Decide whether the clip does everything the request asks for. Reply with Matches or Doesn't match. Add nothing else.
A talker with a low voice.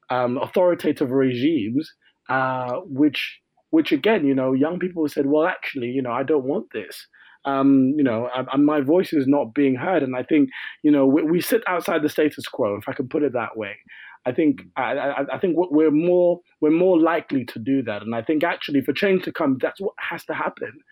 Doesn't match